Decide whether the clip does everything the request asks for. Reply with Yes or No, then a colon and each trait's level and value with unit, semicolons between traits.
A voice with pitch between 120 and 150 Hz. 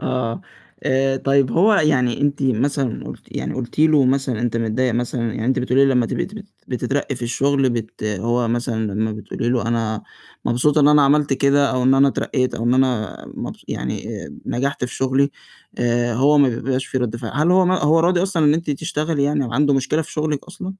Yes: low, 135 Hz